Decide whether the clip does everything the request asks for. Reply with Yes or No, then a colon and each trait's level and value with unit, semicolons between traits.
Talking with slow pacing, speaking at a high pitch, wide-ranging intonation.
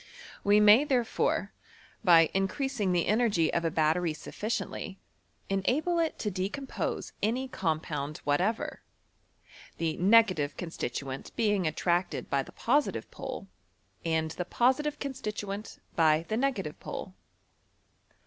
Yes: slow, 120 wpm; high, 195 Hz; wide, 6.2 semitones